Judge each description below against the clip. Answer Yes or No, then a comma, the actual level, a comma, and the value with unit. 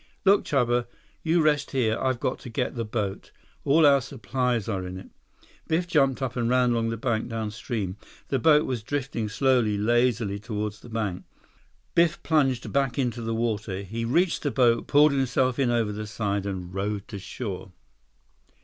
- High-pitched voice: No, low, 120 Hz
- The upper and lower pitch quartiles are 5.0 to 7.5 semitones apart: No, average, 4.0 semitones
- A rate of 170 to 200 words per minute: Yes, average, 175 wpm